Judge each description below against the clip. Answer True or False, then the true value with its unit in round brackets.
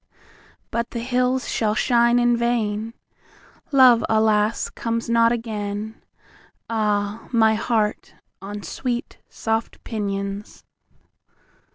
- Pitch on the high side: True (225 Hz)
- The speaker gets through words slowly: True (85 wpm)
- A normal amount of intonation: False (2.1 semitones)